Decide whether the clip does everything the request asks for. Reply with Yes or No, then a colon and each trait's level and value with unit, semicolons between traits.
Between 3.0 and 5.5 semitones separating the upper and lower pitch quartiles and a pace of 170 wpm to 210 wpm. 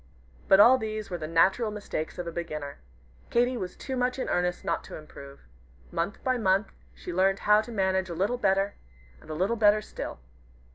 Yes: average, 4.1 semitones; average, 200 wpm